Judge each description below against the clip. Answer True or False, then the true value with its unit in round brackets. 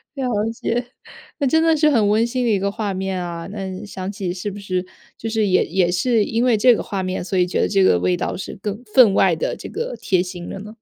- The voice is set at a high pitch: True (200 Hz)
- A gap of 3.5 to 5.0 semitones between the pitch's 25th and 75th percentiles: True (3.8 semitones)